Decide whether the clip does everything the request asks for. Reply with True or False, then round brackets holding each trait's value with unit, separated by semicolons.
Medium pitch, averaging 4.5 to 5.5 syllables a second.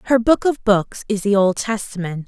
False (210 Hz; 5.0 syllables/s)